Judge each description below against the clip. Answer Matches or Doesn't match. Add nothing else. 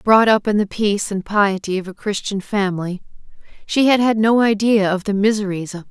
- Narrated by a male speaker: Doesn't match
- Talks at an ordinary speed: Doesn't match